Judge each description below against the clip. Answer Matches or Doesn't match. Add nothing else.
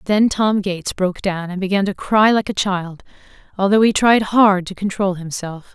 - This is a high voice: Matches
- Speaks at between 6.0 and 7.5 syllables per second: Doesn't match